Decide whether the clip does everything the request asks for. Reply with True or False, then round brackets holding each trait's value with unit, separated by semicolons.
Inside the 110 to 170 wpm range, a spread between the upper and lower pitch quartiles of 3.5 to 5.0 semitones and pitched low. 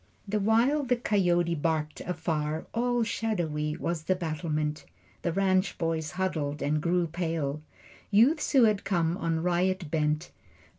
False (140 wpm; 4.1 semitones; 170 Hz)